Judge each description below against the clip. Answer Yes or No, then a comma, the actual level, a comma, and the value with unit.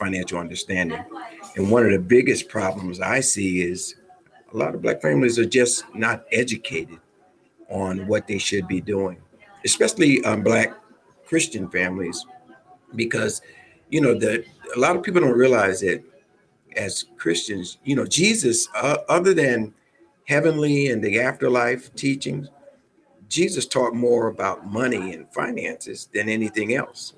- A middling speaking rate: Yes, average, 145 wpm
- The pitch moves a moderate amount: No, wide, 6.5 semitones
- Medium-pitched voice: No, low, 120 Hz